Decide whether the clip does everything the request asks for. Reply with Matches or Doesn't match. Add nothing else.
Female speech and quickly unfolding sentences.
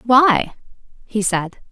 Doesn't match